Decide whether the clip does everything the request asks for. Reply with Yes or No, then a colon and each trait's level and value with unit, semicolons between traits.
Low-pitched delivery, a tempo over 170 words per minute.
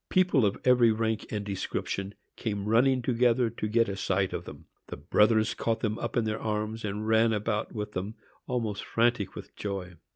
Yes: low, 110 Hz; average, 190 wpm